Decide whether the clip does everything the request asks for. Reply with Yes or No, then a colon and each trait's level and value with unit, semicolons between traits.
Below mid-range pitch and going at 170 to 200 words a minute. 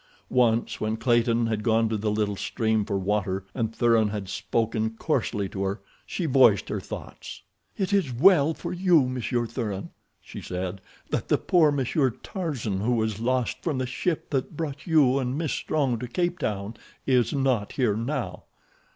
Yes: low, 120 Hz; average, 175 wpm